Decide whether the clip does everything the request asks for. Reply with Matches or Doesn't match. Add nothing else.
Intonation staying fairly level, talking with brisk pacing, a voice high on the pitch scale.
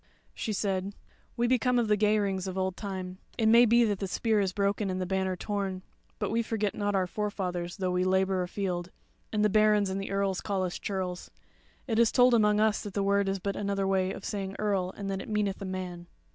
Matches